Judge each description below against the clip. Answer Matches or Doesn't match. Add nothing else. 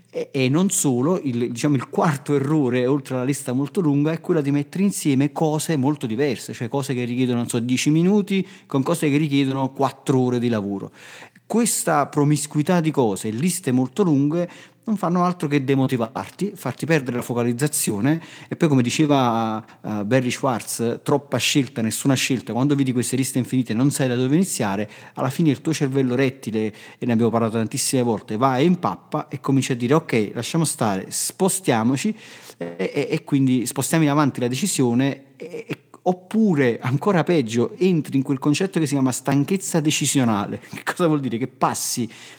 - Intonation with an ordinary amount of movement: Matches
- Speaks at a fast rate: Matches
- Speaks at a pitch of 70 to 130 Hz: Doesn't match